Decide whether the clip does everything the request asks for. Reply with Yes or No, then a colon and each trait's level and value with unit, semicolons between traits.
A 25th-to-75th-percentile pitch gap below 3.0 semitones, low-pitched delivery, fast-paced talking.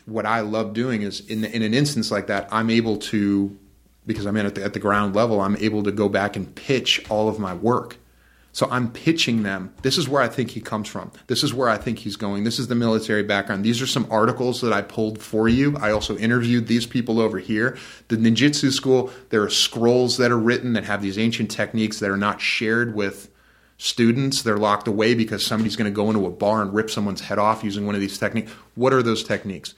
Yes: narrow, 2.4 semitones; low, 110 Hz; fast, 240 wpm